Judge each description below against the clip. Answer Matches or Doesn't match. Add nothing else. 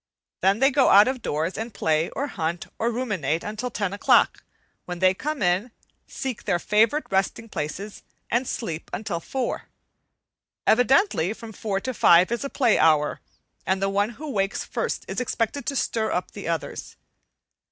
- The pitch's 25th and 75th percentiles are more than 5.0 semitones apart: Matches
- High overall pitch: Matches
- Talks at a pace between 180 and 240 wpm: Doesn't match